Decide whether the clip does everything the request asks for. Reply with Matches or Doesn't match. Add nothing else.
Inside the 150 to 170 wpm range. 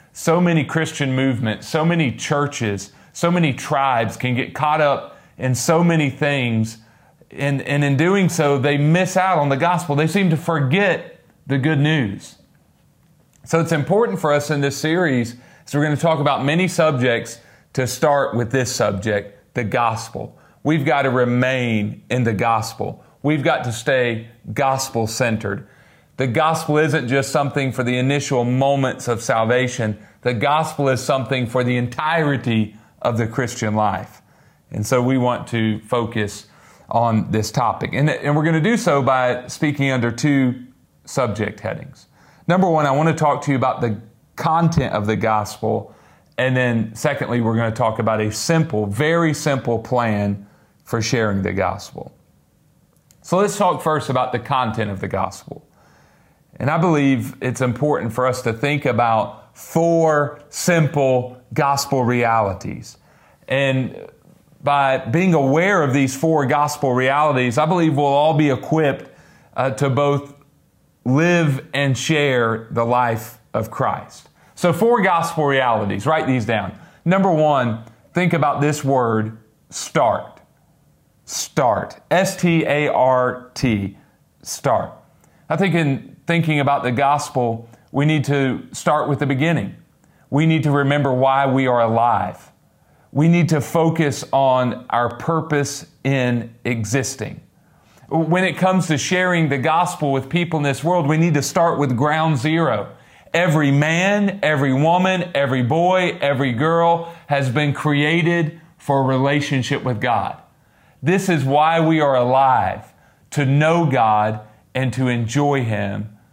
Matches